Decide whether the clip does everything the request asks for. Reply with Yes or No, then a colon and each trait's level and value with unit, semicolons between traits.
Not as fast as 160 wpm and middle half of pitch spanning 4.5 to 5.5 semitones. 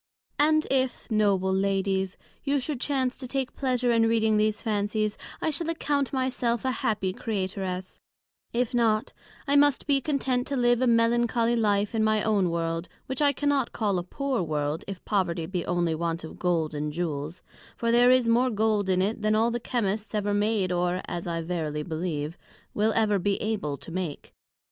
No: average, 185 wpm; average, 5.1 semitones